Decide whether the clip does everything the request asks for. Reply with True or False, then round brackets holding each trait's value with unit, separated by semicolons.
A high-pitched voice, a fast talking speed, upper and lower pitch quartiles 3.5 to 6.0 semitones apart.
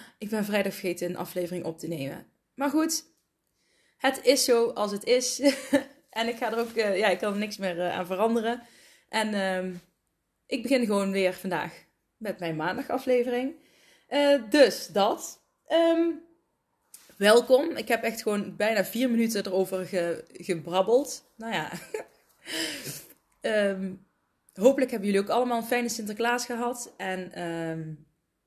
False (220 Hz; 145 wpm; 5.0 semitones)